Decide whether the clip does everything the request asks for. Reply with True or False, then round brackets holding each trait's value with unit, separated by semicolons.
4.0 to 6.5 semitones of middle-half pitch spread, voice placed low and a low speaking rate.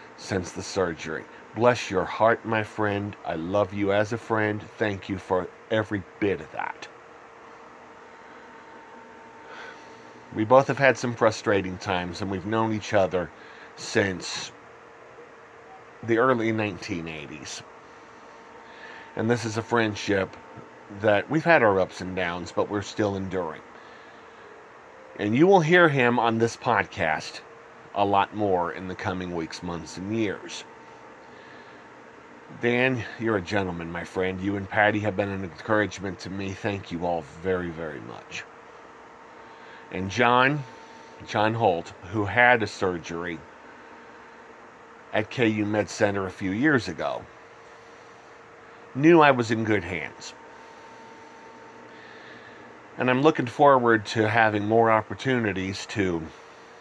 False (3.5 semitones; 105 Hz; 130 wpm)